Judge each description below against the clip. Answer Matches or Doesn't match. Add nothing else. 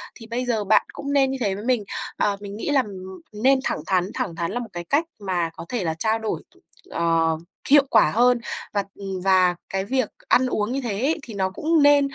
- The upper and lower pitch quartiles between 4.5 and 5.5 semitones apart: Matches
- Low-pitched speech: Doesn't match